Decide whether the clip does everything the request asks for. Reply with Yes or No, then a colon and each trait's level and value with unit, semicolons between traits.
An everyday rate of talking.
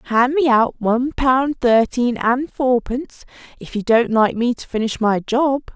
Yes: average, 175 wpm